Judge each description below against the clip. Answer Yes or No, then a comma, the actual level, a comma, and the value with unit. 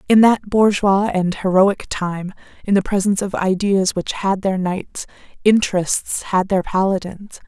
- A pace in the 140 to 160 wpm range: Yes, average, 150 wpm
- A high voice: Yes, high, 195 Hz